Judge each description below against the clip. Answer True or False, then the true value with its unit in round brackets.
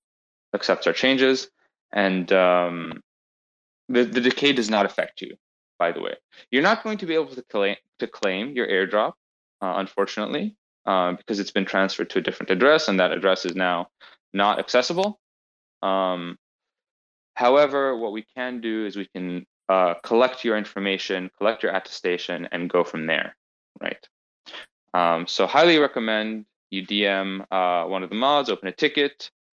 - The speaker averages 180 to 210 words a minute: False (165 wpm)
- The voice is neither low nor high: False (100 Hz)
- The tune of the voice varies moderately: False (5.8 semitones)